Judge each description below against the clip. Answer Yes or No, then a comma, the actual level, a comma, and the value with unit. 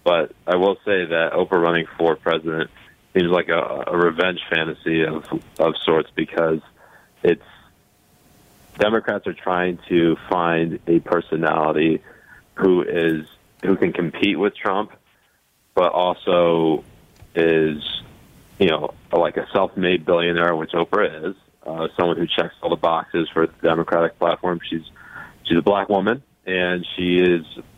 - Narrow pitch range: Yes, narrow, 1.6 semitones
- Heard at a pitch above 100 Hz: No, very low, 85 Hz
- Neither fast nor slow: Yes, average, 145 wpm